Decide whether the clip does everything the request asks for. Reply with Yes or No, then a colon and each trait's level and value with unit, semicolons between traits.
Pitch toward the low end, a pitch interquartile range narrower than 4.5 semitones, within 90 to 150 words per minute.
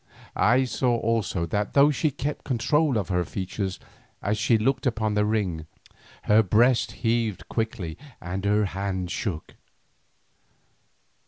Yes: low, 105 Hz; average, 3.9 semitones; slow, 135 wpm